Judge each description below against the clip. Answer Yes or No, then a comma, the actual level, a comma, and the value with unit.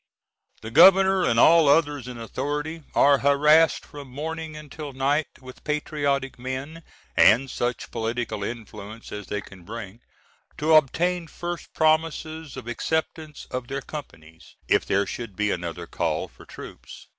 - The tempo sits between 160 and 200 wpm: No, average, 145 wpm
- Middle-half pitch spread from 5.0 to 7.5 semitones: Yes, wide, 5.4 semitones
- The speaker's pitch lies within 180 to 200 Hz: No, medium, 140 Hz